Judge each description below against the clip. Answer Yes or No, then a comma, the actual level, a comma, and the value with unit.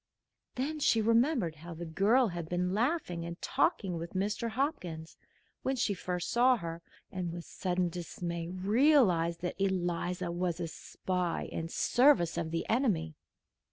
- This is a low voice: No, medium, 180 Hz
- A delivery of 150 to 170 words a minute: Yes, average, 155 wpm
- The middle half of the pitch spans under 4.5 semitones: No, average, 5.2 semitones